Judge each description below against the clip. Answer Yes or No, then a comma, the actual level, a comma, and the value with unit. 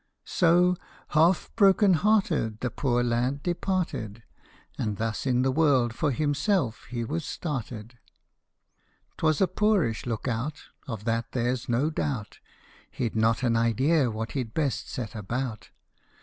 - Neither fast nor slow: Yes, average, 150 wpm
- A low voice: Yes, low, 130 Hz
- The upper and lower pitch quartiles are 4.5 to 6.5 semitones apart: Yes, wide, 5.6 semitones